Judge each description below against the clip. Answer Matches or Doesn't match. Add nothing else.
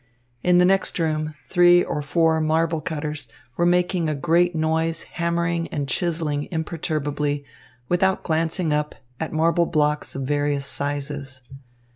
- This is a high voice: Doesn't match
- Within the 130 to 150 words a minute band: Matches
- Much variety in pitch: Doesn't match